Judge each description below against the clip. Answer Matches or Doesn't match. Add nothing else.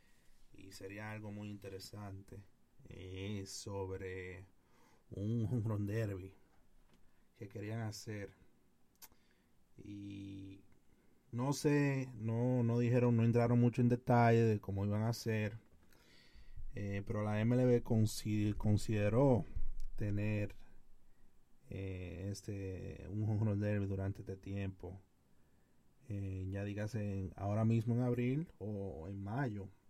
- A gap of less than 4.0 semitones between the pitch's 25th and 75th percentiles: Matches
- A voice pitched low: Matches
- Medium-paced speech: Doesn't match